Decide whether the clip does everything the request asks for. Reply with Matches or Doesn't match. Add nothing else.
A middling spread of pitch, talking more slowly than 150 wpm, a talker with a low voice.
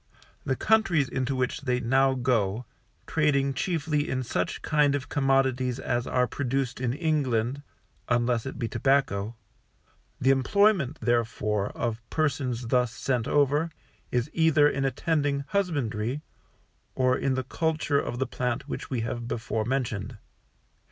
Matches